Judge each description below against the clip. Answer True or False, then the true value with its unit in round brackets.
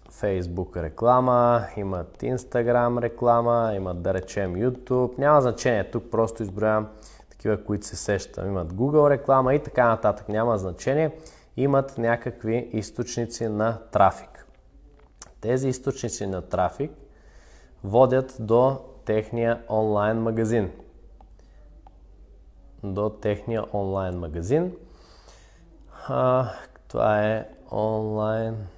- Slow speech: True (100 wpm)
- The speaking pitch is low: True (115 Hz)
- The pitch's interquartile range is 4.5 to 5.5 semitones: False (3.2 semitones)